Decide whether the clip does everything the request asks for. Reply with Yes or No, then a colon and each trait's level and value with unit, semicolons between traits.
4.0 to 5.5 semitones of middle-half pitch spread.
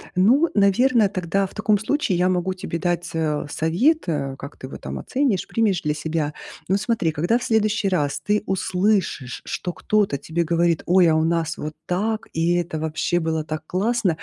Yes: average, 4.6 semitones